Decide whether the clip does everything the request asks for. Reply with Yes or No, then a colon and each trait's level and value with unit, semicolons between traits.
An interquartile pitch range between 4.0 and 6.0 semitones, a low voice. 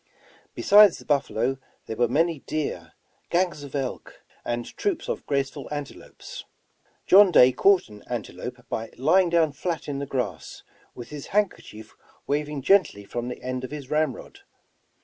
No: average, 5.1 semitones; medium, 145 Hz